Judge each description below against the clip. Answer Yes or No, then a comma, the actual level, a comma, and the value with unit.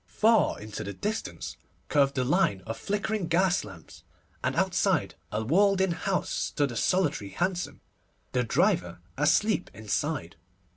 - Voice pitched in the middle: Yes, medium, 150 Hz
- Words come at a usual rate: Yes, average, 145 wpm